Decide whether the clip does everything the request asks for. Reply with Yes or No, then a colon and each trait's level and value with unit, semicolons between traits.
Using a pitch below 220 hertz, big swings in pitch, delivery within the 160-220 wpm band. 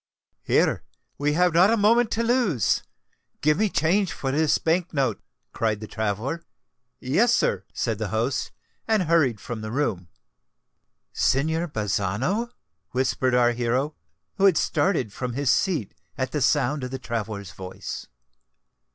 No: medium, 140 Hz; wide, 7.2 semitones; average, 140 wpm